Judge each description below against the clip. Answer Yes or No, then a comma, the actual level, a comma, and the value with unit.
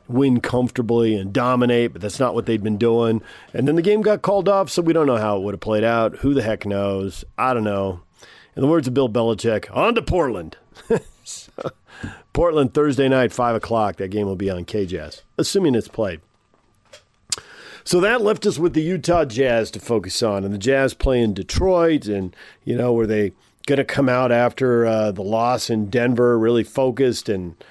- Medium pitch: No, low, 115 Hz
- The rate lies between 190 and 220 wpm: Yes, average, 200 wpm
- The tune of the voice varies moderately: Yes, average, 4.2 semitones